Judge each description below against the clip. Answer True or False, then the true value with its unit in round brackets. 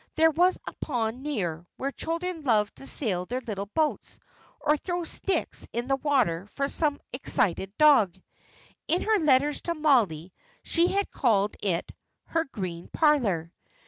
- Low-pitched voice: False (265 Hz)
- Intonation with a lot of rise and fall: True (7.5 semitones)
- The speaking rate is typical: True (150 wpm)